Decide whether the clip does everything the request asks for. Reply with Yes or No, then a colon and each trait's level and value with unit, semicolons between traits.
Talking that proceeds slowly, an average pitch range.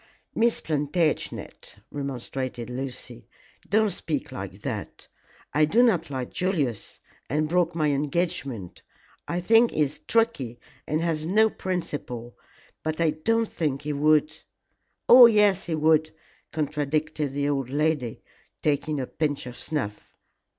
Yes: slow, 130 wpm; average, 3.7 semitones